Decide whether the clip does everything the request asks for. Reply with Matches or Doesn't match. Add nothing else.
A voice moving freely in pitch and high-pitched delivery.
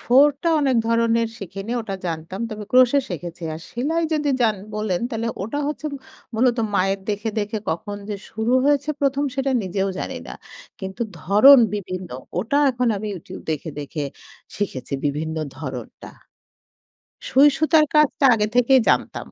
Matches